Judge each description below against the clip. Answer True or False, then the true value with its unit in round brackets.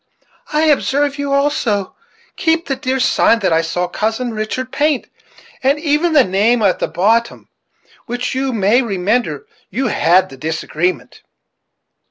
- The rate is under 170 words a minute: True (150 wpm)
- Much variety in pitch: True (6.3 semitones)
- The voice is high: True (245 Hz)